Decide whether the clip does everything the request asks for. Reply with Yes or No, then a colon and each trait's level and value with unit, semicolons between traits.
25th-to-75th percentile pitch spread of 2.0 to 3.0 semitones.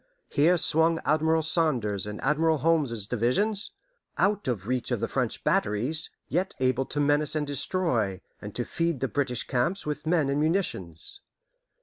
No: average, 5.0 semitones